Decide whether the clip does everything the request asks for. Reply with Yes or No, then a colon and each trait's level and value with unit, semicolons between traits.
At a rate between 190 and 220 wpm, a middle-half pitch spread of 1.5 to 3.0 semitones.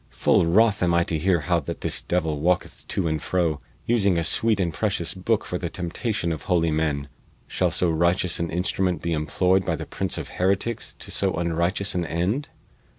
Yes: average, 200 wpm; narrow, 2.5 semitones